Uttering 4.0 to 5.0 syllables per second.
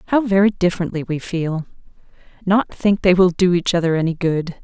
No: 5.7 syllables/s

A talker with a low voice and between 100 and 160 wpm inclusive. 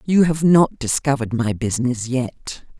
Yes: low, 130 Hz; average, 150 wpm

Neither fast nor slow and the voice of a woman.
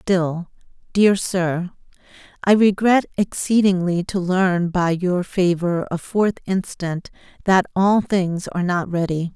No: slow, 120 wpm; female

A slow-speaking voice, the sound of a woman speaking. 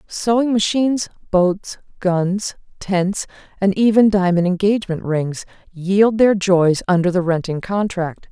Yes: slow, 125 wpm; female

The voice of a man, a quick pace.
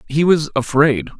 No: male; average, 150 wpm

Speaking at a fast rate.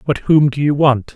Yes: fast, 260 wpm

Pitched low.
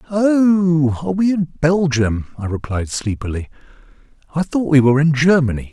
No: medium, 150 Hz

